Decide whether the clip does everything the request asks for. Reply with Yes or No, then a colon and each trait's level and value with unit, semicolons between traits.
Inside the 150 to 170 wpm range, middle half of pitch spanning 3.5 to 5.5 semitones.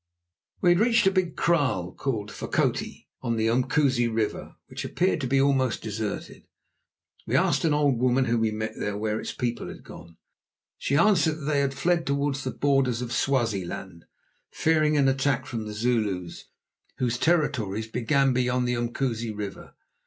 Yes: average, 165 wpm; average, 4.2 semitones